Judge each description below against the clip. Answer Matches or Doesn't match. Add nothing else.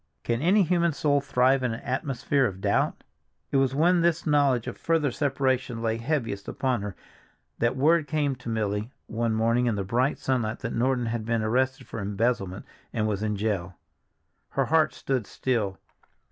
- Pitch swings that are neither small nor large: Matches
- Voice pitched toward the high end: Doesn't match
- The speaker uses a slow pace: Doesn't match